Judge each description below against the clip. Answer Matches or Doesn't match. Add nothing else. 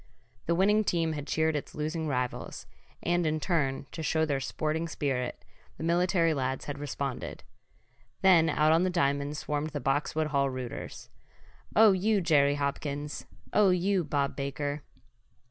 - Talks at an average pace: Matches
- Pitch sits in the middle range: Matches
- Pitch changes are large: Doesn't match